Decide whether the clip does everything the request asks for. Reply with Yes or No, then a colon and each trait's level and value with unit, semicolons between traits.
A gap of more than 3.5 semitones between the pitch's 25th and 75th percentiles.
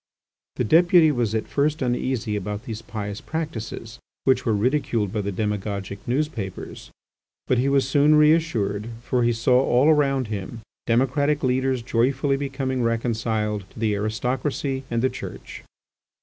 Yes: average, 4.0 semitones